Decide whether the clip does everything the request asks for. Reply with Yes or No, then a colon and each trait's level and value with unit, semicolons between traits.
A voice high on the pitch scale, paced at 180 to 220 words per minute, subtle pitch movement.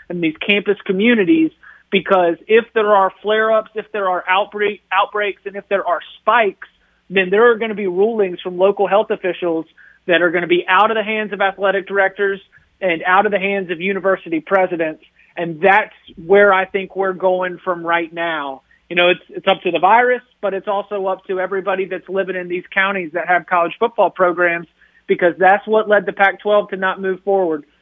Yes: high, 195 Hz; fast, 205 wpm; narrow, 2.1 semitones